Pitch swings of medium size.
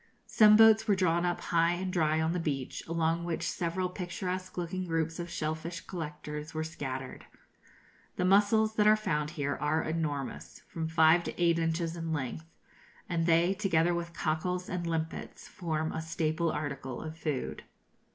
No: narrow, 2.3 semitones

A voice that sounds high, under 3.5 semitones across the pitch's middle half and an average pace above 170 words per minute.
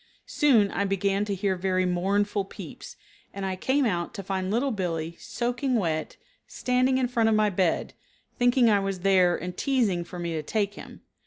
No: high, 200 Hz; average, 4.3 semitones; average, 185 wpm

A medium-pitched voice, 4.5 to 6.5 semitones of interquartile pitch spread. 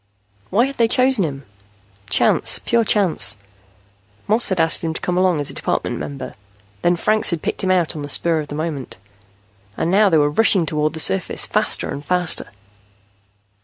Yes: medium, 170 Hz; average, 4.9 semitones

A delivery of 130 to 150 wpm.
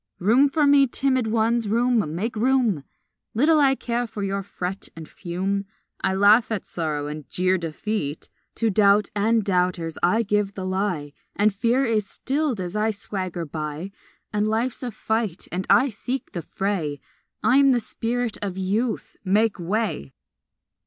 No: average, 160 wpm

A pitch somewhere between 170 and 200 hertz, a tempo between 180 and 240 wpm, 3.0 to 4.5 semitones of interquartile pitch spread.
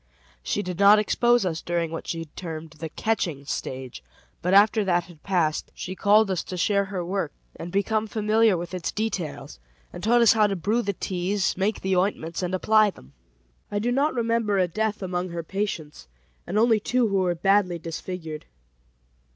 Yes: high, 190 Hz; average, 185 wpm; average, 3.6 semitones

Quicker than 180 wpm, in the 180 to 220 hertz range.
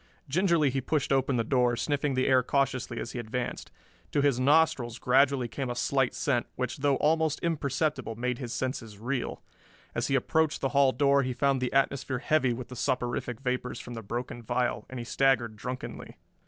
No: average, 190 wpm; low, 130 Hz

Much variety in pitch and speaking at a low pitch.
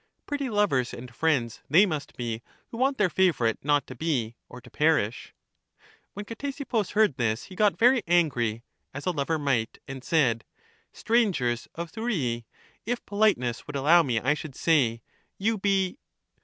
No: wide, 8.9 semitones; medium, 155 Hz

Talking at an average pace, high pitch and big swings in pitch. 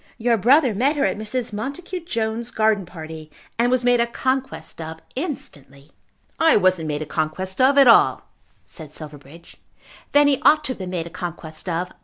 Yes: average, 185 wpm; high, 215 Hz; wide, 8.0 semitones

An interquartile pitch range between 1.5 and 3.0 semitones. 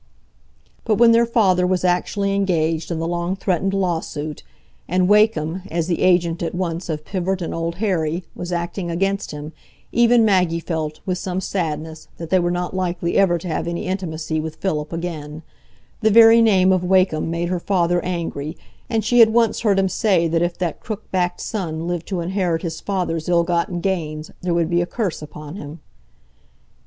Yes: narrow, 2.6 semitones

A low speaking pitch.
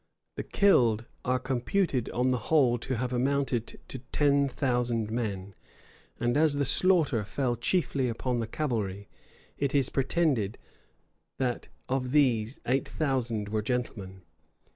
Yes: low, 125 Hz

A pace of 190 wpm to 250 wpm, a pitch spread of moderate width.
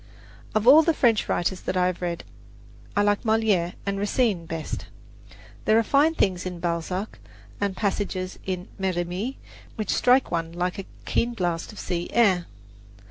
No: average, 160 wpm; average, 3.8 semitones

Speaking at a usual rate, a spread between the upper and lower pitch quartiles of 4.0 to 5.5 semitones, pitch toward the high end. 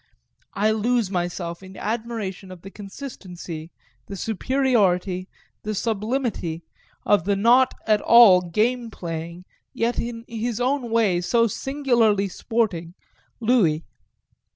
No: slow, 115 wpm; average, 4.5 semitones; high, 210 Hz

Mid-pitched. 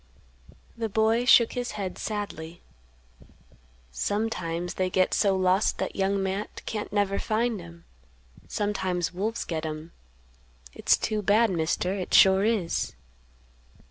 No: high, 195 Hz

